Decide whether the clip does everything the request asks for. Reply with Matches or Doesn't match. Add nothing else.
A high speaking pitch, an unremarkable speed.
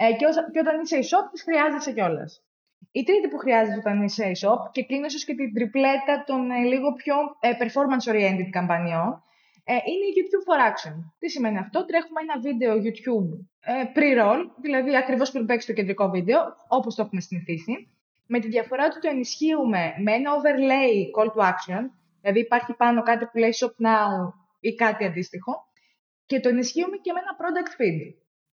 Doesn't match